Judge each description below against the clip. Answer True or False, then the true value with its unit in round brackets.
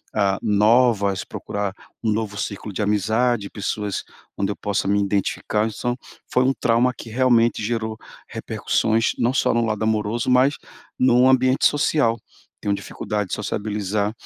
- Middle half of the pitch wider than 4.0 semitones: False (2.8 semitones)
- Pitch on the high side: False (110 Hz)